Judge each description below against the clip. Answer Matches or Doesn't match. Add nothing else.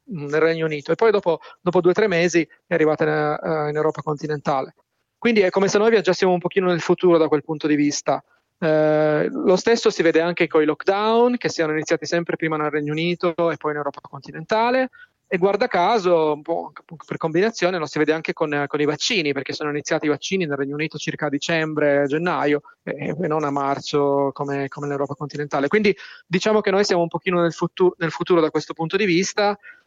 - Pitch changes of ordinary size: Matches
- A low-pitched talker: Doesn't match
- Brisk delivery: Matches